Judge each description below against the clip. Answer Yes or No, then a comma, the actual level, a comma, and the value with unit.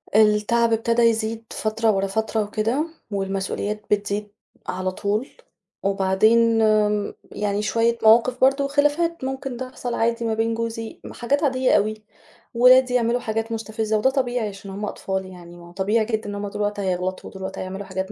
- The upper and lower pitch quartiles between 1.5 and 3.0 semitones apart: Yes, narrow, 2.6 semitones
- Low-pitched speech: No, high, 220 Hz